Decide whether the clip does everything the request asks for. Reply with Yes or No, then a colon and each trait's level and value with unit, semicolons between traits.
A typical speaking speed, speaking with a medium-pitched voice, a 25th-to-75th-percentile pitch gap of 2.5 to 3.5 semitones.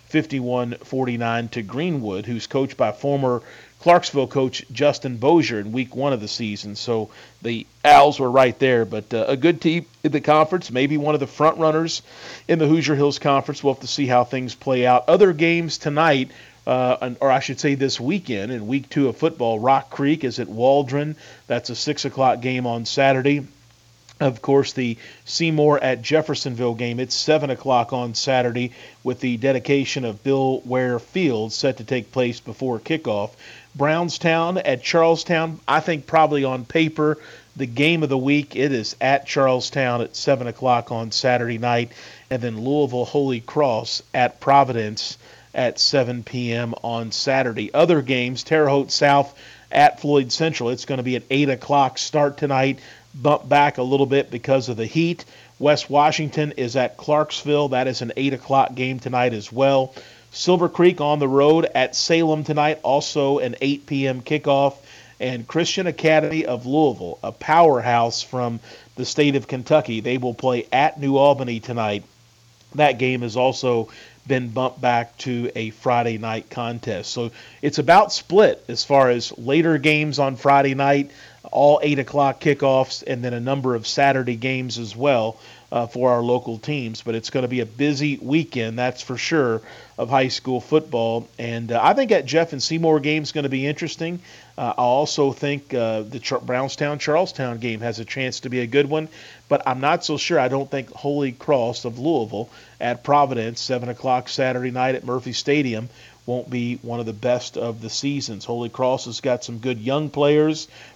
No: average, 180 wpm; low, 130 Hz; average, 3.2 semitones